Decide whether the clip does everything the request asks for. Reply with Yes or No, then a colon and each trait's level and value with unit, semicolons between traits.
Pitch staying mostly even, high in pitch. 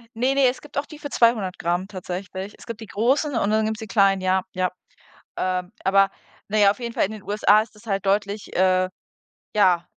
No: average, 3.1 semitones; high, 205 Hz